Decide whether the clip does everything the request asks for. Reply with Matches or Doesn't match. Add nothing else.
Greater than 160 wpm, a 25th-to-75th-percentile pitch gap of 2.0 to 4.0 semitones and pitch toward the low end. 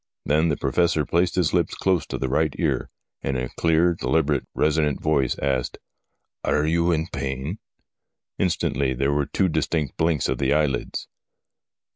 Matches